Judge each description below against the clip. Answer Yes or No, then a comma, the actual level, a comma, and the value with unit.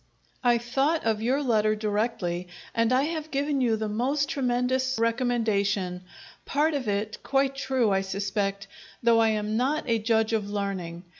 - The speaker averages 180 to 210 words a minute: No, average, 160 wpm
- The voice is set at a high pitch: Yes, high, 230 Hz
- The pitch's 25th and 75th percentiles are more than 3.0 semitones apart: Yes, average, 4.0 semitones